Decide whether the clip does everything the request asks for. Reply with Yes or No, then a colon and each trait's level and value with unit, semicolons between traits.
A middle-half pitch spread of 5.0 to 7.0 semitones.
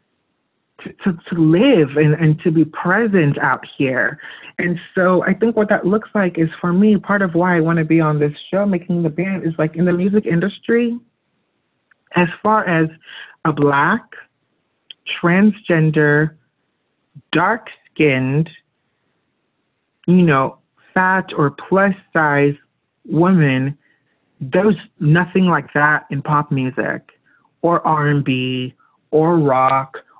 No: average, 4.1 semitones